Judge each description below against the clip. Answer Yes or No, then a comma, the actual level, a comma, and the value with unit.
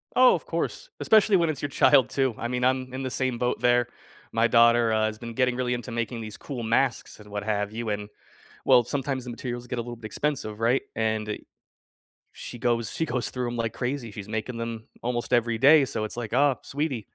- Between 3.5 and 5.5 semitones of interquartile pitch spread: No, narrow, 2.5 semitones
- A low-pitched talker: Yes, low, 120 Hz